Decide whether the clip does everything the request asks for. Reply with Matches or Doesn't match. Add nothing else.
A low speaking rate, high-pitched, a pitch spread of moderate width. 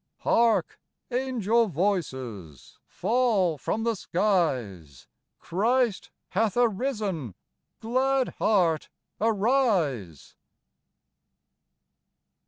Doesn't match